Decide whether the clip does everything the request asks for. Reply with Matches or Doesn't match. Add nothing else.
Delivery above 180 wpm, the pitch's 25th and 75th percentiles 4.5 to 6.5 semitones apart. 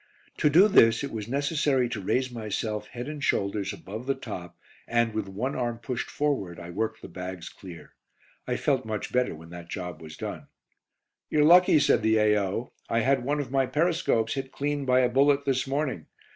Matches